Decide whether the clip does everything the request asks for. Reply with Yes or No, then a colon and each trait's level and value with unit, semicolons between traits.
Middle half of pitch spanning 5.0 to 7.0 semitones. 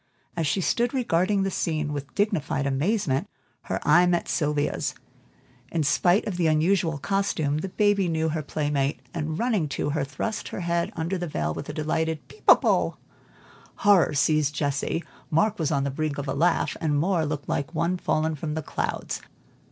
No: average, 3.4 semitones